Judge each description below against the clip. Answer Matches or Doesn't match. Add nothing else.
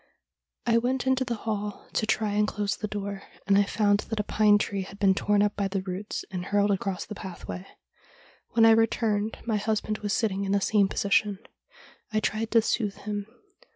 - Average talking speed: Doesn't match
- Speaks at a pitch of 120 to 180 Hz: Doesn't match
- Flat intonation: Matches